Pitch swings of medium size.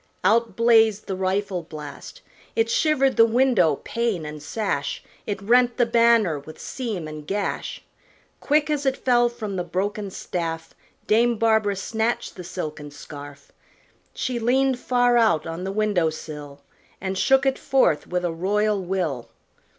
No: wide, 5.9 semitones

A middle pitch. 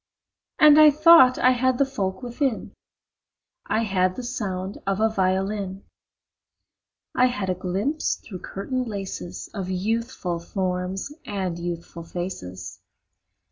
No: high, 195 Hz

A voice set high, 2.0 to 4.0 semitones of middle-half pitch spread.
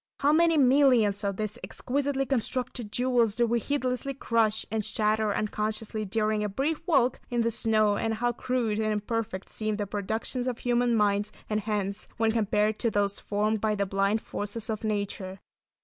Yes: high, 220 Hz; average, 2.7 semitones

